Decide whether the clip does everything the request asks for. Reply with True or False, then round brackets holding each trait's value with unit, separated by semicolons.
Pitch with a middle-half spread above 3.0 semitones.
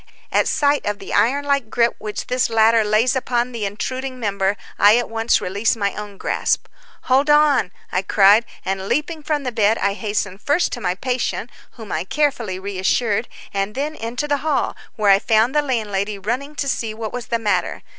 True (4.3 semitones)